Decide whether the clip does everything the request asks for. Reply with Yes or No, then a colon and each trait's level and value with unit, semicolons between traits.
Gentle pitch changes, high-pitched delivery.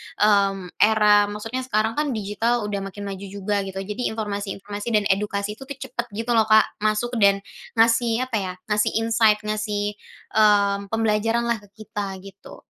Yes: narrow, 1.9 semitones; high, 210 Hz